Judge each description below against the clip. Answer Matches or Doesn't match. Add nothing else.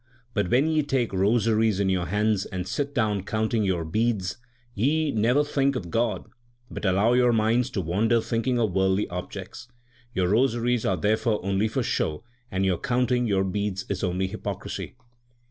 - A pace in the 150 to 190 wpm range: Matches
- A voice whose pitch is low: Matches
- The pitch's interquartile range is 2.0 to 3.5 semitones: Doesn't match